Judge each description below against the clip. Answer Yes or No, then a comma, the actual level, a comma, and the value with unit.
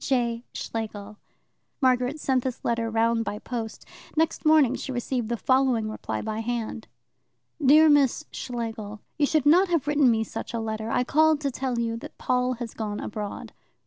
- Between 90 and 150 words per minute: No, average, 175 wpm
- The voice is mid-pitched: No, high, 240 Hz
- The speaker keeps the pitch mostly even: No, average, 3.3 semitones